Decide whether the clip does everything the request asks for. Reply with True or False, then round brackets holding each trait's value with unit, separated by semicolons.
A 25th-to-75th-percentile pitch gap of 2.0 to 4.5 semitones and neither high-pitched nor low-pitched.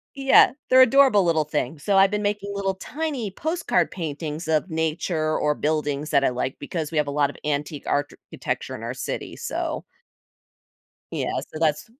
False (5.3 semitones; 160 Hz)